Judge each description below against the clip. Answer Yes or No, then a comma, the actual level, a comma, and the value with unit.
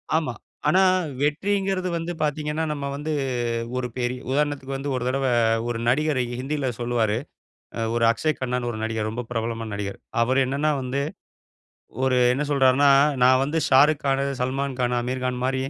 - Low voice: Yes, low, 130 Hz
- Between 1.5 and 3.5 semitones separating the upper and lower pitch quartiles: Yes, average, 3.2 semitones